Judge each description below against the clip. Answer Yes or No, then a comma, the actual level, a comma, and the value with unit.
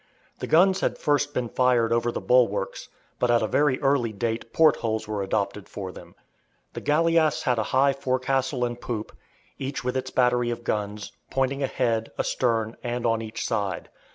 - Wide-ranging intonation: No, average, 3.0 semitones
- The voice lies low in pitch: Yes, low, 120 Hz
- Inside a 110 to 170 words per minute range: No, average, 180 wpm